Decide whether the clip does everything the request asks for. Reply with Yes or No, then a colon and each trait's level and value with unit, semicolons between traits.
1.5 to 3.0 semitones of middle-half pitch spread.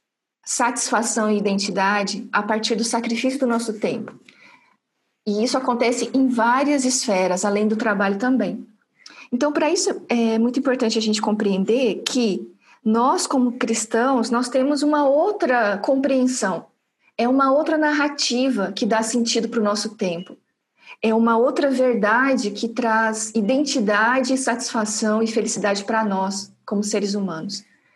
No: average, 3.4 semitones